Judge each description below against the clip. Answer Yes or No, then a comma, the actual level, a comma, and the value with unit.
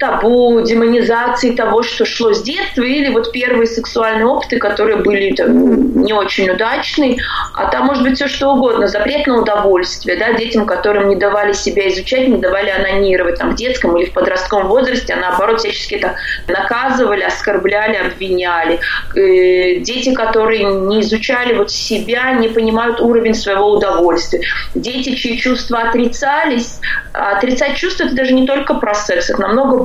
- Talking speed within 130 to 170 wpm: Yes, average, 155 wpm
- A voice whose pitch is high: Yes, high, 230 Hz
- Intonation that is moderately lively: Yes, average, 4.0 semitones